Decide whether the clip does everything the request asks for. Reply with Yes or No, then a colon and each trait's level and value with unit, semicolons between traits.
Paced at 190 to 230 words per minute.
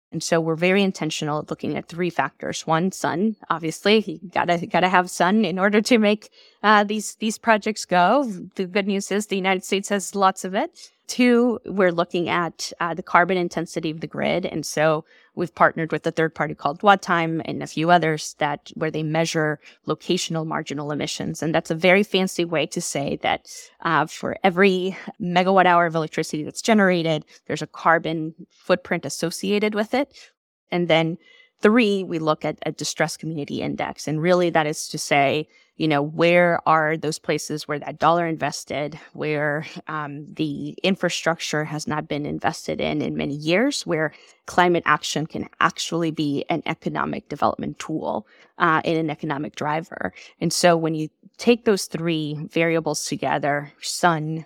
No: average, 175 wpm